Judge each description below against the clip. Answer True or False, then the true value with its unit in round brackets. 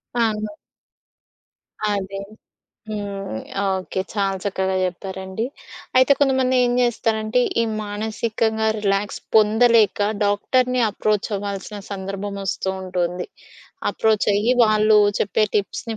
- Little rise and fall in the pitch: True (2.1 semitones)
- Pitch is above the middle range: True (210 Hz)